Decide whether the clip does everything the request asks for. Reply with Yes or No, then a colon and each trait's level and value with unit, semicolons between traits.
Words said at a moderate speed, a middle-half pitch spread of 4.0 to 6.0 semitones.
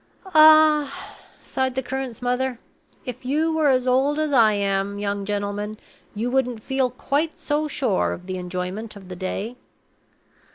Yes: average, 155 wpm; wide, 5.4 semitones